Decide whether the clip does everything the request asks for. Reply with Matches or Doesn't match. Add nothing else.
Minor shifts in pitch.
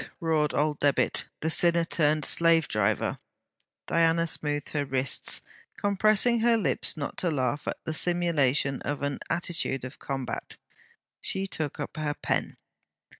Doesn't match